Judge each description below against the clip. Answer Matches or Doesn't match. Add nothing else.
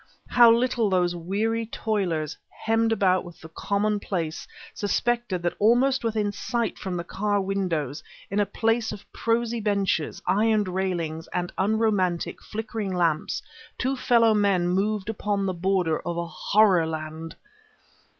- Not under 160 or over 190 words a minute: Doesn't match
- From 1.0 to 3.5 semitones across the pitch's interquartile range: Doesn't match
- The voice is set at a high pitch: Matches